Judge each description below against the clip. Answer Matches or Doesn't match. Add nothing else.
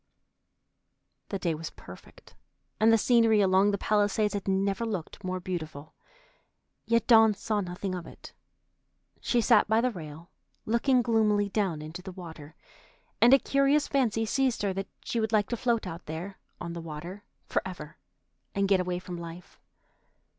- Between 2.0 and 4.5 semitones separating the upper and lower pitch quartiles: Matches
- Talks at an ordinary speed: Matches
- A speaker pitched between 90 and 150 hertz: Doesn't match